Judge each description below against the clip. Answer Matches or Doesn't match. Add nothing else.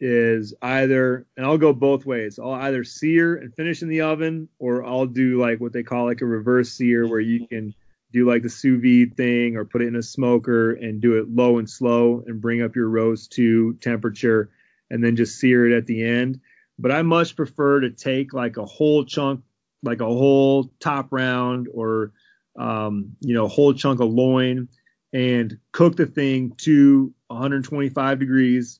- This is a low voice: Matches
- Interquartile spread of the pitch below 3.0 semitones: Matches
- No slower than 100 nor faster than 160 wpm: Doesn't match